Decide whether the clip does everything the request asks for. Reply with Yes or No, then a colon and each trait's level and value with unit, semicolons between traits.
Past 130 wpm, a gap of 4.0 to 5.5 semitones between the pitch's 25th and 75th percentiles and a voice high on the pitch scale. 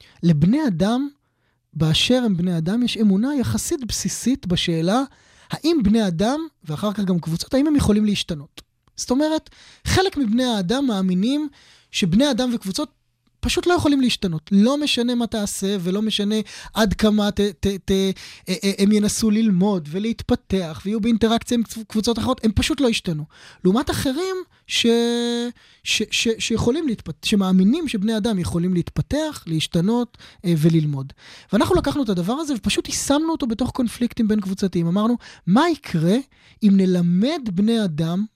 Yes: average, 145 wpm; average, 5.0 semitones; high, 215 Hz